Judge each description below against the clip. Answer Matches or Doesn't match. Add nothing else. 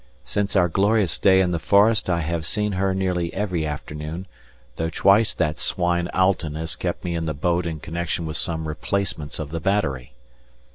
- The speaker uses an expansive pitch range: Doesn't match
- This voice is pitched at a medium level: Doesn't match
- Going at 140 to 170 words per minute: Doesn't match